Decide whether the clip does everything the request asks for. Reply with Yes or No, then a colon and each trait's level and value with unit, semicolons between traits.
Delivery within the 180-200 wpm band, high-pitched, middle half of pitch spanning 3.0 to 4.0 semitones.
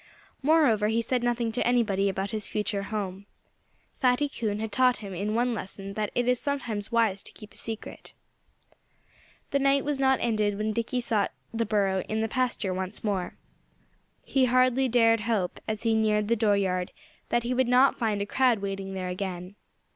Yes: average, 185 wpm; high, 220 Hz; average, 3.5 semitones